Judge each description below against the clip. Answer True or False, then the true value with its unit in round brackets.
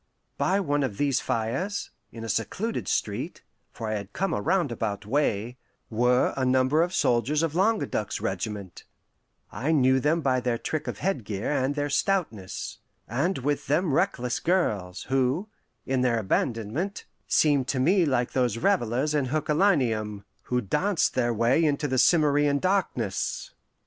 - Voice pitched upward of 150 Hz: False (130 Hz)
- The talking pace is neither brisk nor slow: True (150 wpm)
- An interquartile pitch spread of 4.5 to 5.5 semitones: True (5.2 semitones)